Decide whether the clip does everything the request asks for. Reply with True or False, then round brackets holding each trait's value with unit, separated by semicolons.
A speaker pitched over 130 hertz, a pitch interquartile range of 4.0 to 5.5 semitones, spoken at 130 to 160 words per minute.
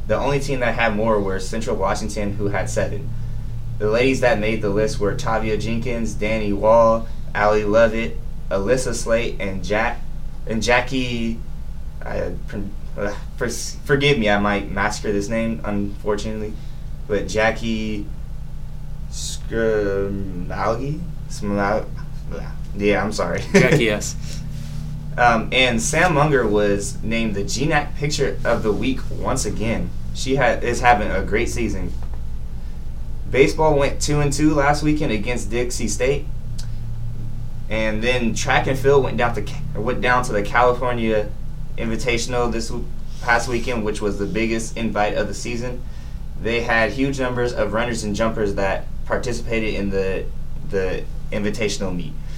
False (115 Hz; 4.4 semitones; 140 wpm)